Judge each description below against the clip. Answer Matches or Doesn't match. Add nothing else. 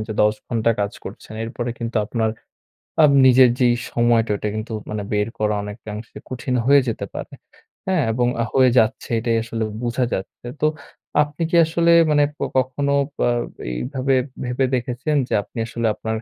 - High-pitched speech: Doesn't match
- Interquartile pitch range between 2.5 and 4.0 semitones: Matches